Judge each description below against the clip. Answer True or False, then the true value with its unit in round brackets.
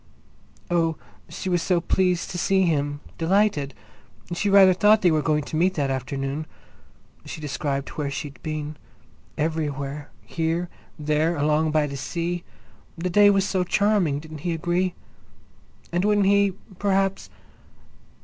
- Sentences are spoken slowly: True (130 wpm)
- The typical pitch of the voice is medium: True (165 Hz)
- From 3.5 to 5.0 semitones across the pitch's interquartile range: True (3.9 semitones)